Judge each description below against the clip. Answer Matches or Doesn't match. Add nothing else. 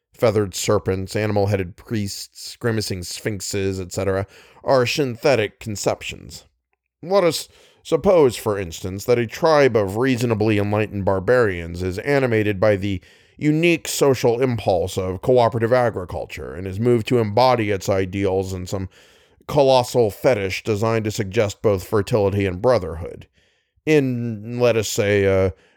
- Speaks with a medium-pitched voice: Doesn't match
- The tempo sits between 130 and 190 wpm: Matches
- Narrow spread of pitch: Doesn't match